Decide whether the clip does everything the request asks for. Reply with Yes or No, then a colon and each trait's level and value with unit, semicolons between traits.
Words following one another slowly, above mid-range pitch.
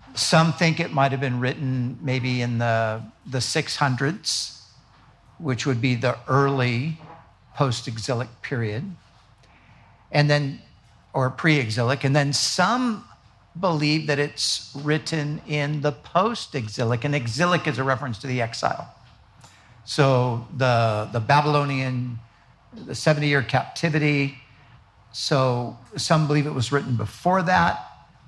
No: slow, 120 wpm; low, 130 Hz